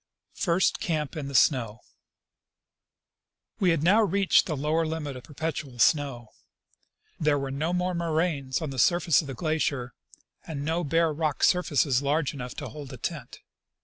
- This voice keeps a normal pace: Yes, average, 160 wpm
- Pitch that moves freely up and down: No, average, 3.2 semitones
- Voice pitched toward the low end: No, medium, 150 Hz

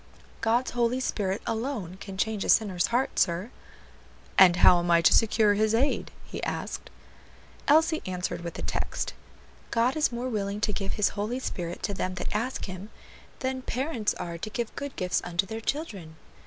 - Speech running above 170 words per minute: Yes, average, 180 wpm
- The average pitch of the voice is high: Yes, high, 210 Hz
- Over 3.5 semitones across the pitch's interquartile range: Yes, average, 4.8 semitones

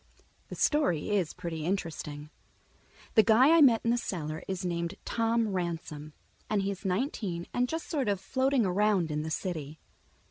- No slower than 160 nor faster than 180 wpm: Yes, average, 170 wpm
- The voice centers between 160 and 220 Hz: Yes, high, 190 Hz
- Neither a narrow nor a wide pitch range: No, wide, 5.7 semitones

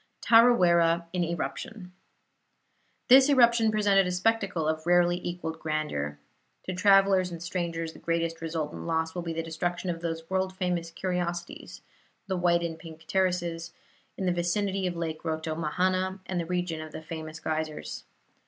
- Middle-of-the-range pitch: Yes, medium, 175 Hz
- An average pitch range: No, narrow, 2.3 semitones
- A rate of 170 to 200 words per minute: No, average, 155 wpm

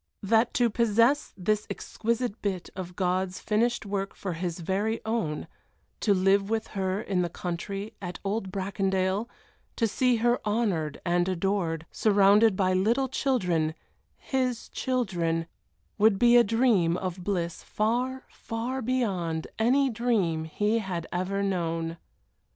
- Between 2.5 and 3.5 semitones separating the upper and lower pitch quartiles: No, average, 4.1 semitones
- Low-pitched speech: No, high, 200 Hz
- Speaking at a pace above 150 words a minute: No, slow, 135 wpm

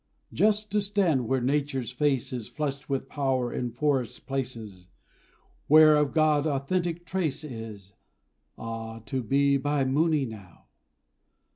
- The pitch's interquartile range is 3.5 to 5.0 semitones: Yes, average, 3.9 semitones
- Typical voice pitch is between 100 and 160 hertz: Yes, low, 135 Hz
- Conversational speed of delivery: No, slow, 130 wpm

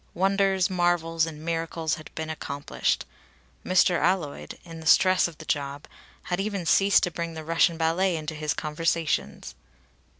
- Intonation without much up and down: Yes, narrow, 2.3 semitones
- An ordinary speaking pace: Yes, average, 155 wpm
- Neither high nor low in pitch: Yes, medium, 165 Hz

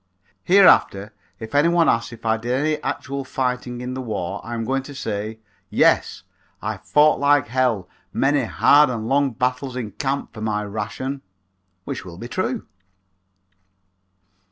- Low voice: Yes, low, 125 Hz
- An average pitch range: Yes, average, 4.0 semitones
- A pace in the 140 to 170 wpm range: Yes, average, 155 wpm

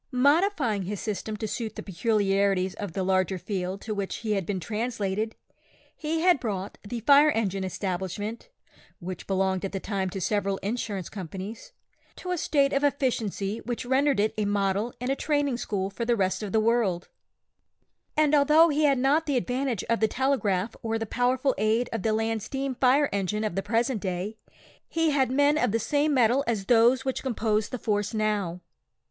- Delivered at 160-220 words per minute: Yes, average, 190 wpm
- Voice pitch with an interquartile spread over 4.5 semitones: Yes, average, 4.9 semitones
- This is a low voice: No, high, 220 Hz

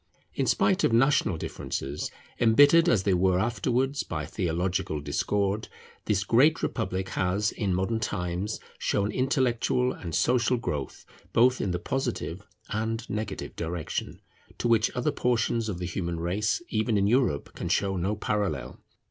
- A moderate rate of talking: Yes, average, 150 wpm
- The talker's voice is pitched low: Yes, low, 105 Hz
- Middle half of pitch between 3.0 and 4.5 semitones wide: No, average, 5.0 semitones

